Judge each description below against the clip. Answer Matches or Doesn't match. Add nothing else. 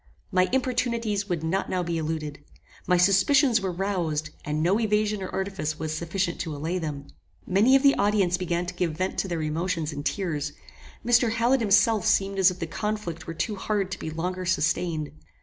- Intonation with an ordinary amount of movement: Matches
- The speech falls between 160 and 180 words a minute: Doesn't match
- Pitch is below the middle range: Doesn't match